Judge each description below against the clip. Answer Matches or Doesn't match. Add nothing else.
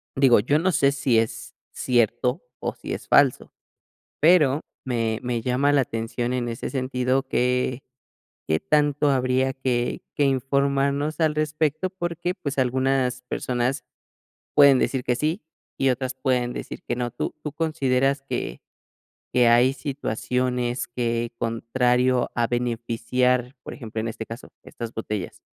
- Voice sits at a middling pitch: Doesn't match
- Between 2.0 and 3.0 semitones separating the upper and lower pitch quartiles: Matches